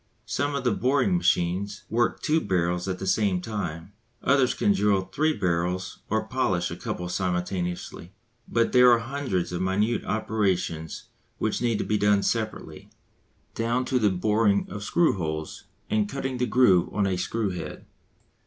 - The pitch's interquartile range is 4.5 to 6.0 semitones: Yes, average, 4.8 semitones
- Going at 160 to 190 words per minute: Yes, average, 165 wpm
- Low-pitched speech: Yes, low, 105 Hz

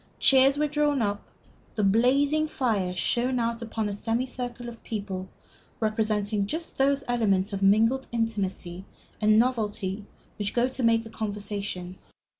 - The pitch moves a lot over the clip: No, average, 3.7 semitones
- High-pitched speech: Yes, high, 225 Hz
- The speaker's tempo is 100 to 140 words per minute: Yes, slow, 135 wpm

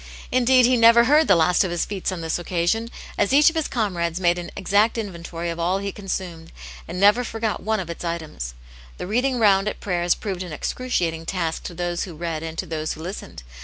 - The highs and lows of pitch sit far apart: No, average, 4.6 semitones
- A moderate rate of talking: No, fast, 220 wpm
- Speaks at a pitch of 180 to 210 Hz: Yes, medium, 185 Hz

